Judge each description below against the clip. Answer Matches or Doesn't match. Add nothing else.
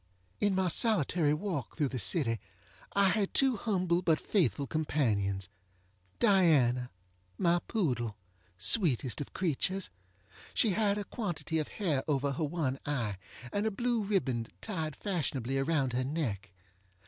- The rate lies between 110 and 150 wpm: Matches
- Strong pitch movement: Matches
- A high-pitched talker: Doesn't match